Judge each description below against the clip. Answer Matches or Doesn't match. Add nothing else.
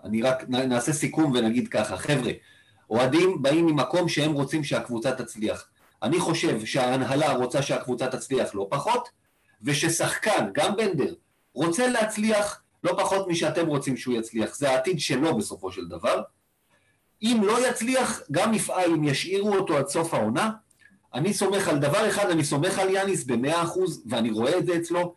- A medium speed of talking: Doesn't match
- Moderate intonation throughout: Doesn't match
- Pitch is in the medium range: Matches